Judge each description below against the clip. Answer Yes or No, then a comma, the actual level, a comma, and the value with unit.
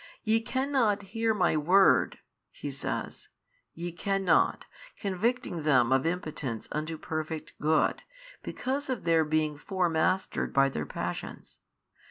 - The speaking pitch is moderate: Yes, medium, 175 Hz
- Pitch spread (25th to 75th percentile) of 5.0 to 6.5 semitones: Yes, wide, 5.4 semitones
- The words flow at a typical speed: No, slow, 125 wpm